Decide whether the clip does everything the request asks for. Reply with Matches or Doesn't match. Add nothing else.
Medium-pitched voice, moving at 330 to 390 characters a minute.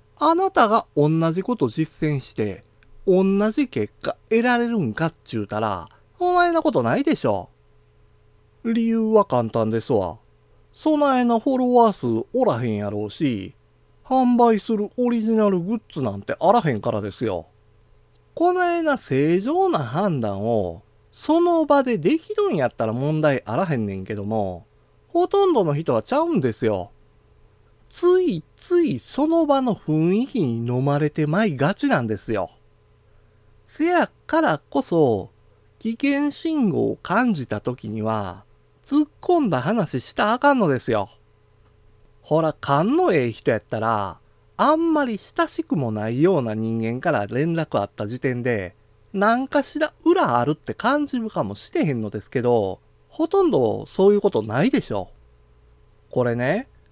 Doesn't match